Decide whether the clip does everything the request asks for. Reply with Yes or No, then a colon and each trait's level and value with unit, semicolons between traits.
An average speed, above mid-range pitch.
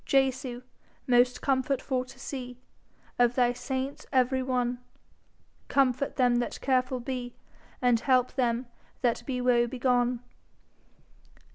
No: slow, 120 wpm; very high, 250 Hz